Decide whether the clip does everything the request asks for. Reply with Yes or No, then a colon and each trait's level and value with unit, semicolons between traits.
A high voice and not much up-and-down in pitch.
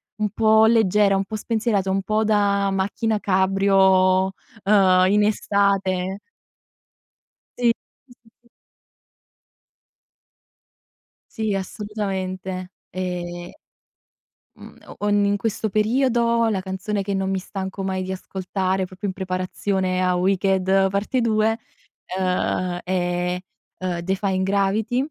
Yes: high, 195 Hz; narrow, 2.0 semitones